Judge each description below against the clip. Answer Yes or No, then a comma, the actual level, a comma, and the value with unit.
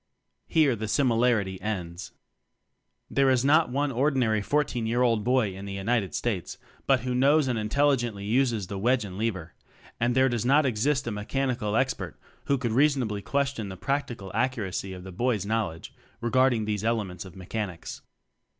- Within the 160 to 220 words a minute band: Yes, average, 175 wpm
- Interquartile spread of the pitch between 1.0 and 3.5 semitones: No, average, 4.3 semitones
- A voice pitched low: Yes, low, 115 Hz